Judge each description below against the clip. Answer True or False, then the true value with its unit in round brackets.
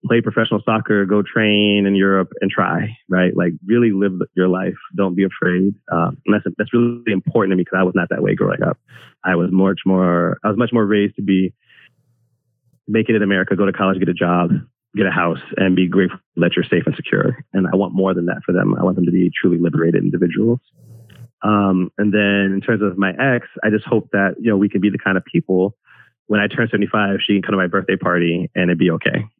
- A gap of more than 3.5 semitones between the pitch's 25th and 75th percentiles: False (2.8 semitones)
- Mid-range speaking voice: False (100 Hz)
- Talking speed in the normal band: False (240 wpm)